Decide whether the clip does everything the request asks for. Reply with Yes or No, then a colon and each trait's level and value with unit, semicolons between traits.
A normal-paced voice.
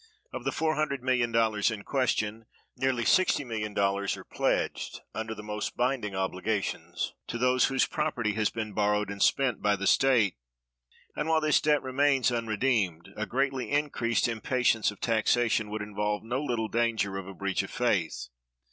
Yes: average, 155 wpm